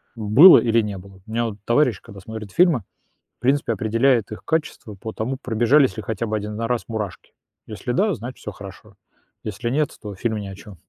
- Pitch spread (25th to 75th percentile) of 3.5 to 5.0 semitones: No, average, 3.1 semitones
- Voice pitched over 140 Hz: No, low, 110 Hz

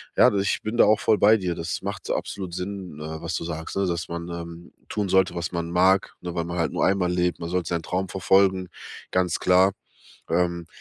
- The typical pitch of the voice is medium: No, very low, 90 Hz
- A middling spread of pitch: No, narrow, 2.0 semitones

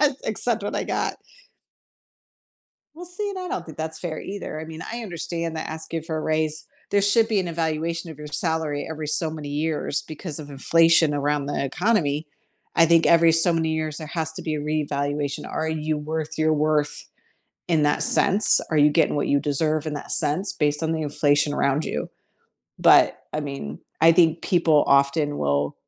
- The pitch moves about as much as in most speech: No, narrow, 2.0 semitones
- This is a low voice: No, medium, 155 Hz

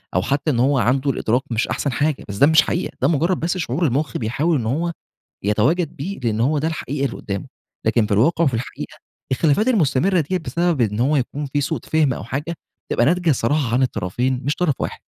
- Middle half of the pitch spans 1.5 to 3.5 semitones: No, average, 4.8 semitones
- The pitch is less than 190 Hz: Yes, medium, 140 Hz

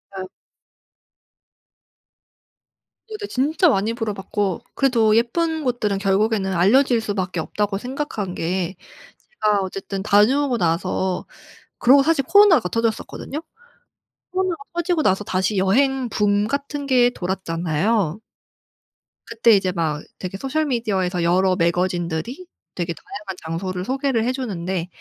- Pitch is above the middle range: Yes, high, 210 Hz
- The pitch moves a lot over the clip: Yes, wide, 5.9 semitones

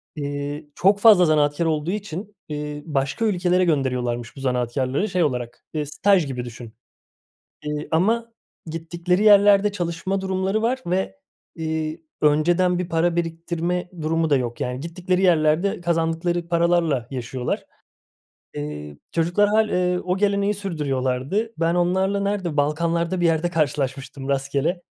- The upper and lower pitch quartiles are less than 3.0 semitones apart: No, average, 4.3 semitones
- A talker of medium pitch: Yes, medium, 165 Hz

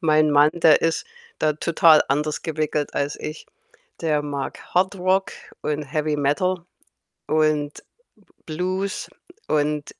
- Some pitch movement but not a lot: No, narrow, 2.3 semitones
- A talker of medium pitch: Yes, medium, 155 Hz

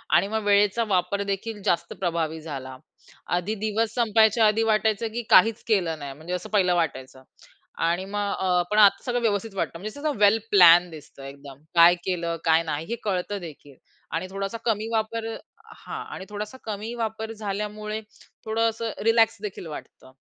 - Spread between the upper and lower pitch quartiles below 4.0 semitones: No, average, 4.4 semitones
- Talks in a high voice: Yes, high, 200 Hz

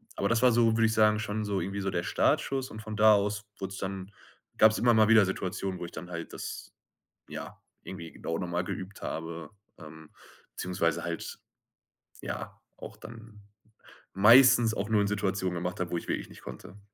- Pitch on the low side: Yes, low, 100 Hz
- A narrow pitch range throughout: No, average, 3.4 semitones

